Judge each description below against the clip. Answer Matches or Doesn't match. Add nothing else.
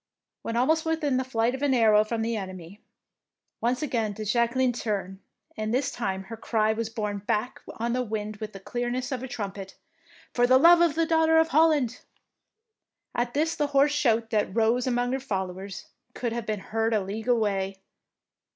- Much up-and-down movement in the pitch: Doesn't match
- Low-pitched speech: Doesn't match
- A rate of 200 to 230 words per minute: Matches